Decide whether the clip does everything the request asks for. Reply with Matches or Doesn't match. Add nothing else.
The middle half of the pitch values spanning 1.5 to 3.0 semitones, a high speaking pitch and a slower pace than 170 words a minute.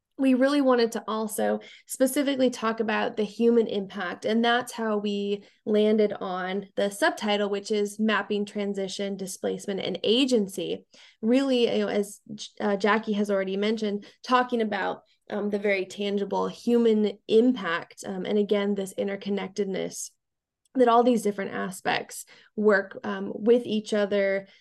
Matches